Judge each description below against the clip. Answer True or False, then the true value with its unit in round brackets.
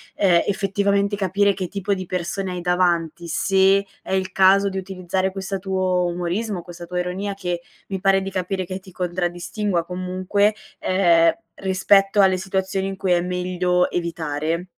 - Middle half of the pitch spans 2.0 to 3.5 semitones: False (1.6 semitones)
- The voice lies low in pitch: False (185 Hz)